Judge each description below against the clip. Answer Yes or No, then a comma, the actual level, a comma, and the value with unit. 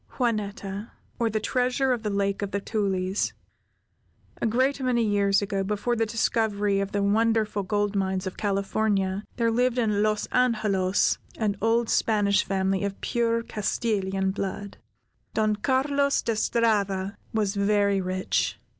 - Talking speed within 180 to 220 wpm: No, average, 145 wpm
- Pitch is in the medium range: No, high, 210 Hz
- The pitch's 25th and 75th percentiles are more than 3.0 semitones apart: No, narrow, 2.6 semitones